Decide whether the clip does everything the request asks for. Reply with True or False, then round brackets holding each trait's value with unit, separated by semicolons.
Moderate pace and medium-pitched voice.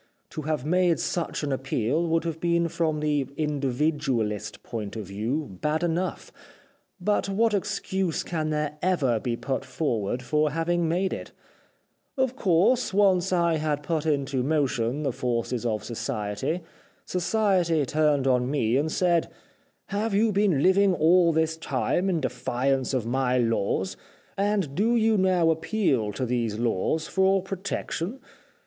True (150 wpm; 155 Hz)